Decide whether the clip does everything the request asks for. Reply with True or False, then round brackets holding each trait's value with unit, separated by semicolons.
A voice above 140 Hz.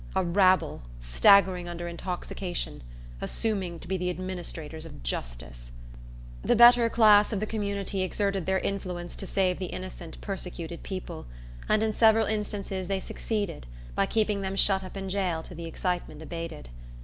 True (185 Hz)